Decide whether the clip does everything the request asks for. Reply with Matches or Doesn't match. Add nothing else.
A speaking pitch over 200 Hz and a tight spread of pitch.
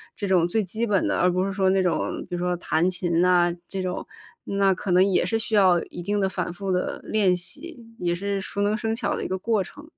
Doesn't match